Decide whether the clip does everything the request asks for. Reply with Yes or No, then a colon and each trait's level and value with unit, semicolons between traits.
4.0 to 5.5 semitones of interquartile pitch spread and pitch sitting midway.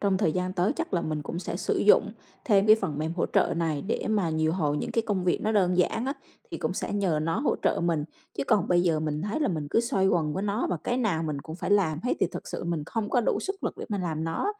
Yes: average, 4.7 semitones; medium, 180 Hz